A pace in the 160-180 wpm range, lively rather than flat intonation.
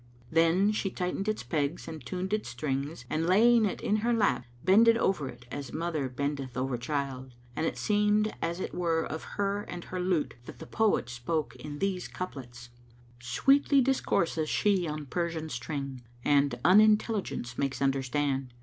Yes: average, 170 wpm; wide, 6.4 semitones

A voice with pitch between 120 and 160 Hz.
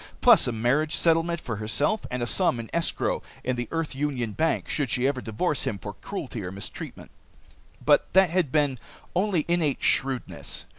Yes: medium, 140 Hz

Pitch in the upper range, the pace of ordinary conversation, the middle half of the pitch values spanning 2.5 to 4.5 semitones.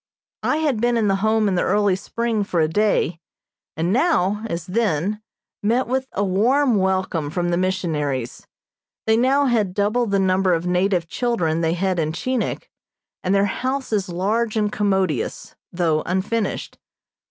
Yes: high, 195 Hz; average, 165 wpm; average, 4.2 semitones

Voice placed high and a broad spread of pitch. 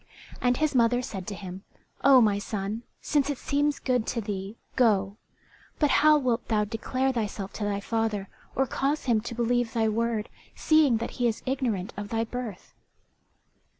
No: high, 230 Hz; average, 3.6 semitones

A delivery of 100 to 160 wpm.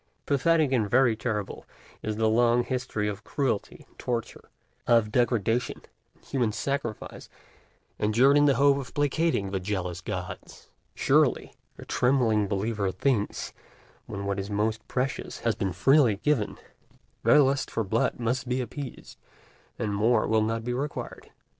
Yes: average, 145 wpm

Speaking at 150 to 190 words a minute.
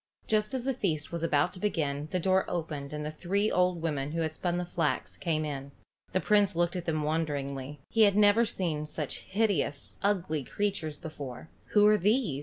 No: average, 200 wpm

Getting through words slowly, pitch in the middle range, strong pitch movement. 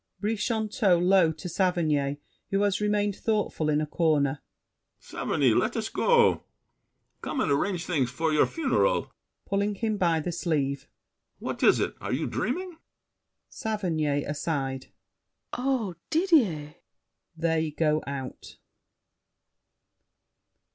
Yes: slow, 115 wpm; medium, 175 Hz; wide, 5.7 semitones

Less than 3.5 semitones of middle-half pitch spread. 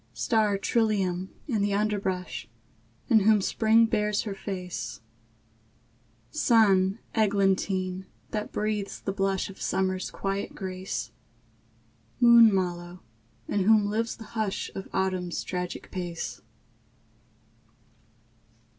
Yes: narrow, 2.5 semitones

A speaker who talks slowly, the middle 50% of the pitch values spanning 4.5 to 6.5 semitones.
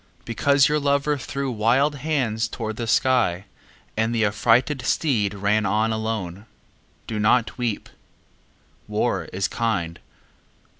No: slow, 120 wpm; average, 3.8 semitones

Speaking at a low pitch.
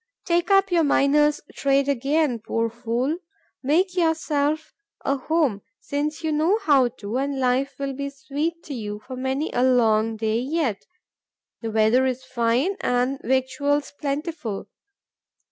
No: very high, 275 Hz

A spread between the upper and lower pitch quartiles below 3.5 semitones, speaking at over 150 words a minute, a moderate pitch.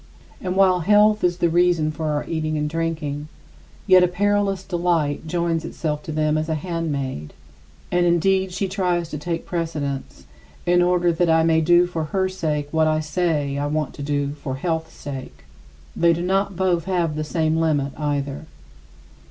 Yes: average, 2.8 semitones; average, 185 wpm; medium, 165 Hz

